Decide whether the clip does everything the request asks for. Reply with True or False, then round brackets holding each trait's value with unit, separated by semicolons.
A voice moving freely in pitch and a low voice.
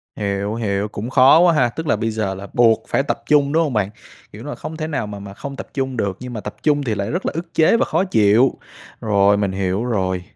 True (5.7 semitones; 115 Hz)